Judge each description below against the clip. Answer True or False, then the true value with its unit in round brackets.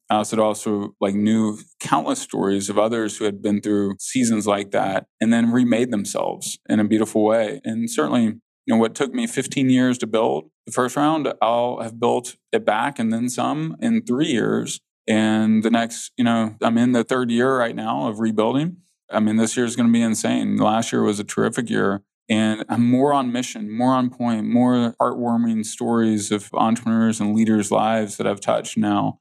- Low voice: True (115 Hz)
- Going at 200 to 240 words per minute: True (205 wpm)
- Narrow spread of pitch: True (2.3 semitones)